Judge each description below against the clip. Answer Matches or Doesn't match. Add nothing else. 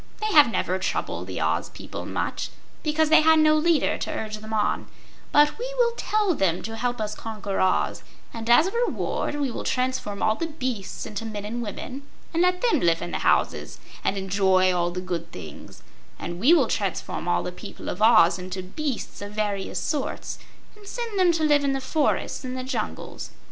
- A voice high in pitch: Matches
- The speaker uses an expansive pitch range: Matches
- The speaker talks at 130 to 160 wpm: Doesn't match